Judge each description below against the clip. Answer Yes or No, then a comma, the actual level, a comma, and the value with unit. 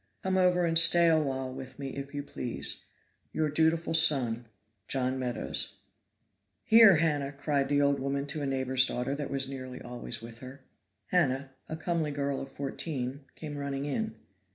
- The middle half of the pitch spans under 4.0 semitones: Yes, average, 3.0 semitones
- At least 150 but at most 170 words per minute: Yes, average, 165 wpm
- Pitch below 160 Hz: Yes, medium, 140 Hz